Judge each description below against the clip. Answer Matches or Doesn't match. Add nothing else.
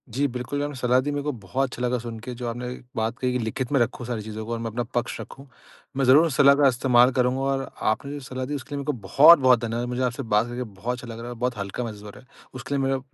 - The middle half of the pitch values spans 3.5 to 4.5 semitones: Doesn't match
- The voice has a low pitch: Matches